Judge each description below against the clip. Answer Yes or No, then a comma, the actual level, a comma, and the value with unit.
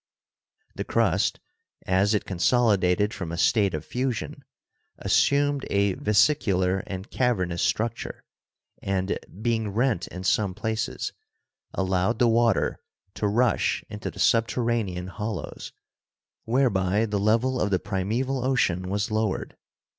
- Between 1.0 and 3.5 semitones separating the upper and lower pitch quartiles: No, average, 3.9 semitones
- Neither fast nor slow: No, slow, 125 wpm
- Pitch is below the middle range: Yes, low, 105 Hz